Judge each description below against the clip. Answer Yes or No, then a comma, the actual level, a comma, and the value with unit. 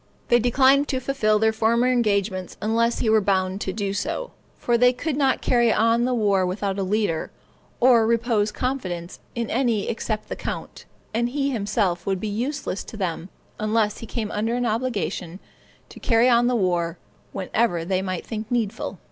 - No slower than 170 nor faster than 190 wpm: Yes, average, 180 wpm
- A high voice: Yes, high, 220 Hz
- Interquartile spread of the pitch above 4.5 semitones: No, average, 3.4 semitones